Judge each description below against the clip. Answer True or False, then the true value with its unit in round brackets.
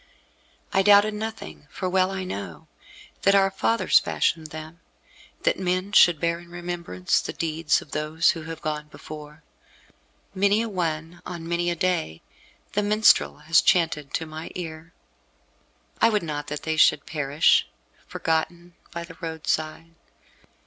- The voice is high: False (165 Hz)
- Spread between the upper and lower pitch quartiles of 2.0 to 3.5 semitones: True (2.9 semitones)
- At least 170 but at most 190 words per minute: False (150 wpm)